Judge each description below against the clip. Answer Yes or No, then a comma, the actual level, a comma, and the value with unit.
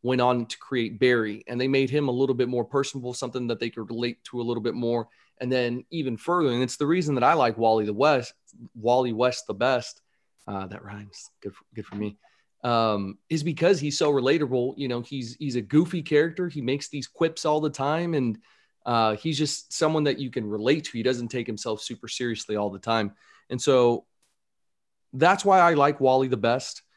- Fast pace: Yes, fast, 220 wpm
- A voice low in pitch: Yes, low, 125 Hz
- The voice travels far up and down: No, average, 3.9 semitones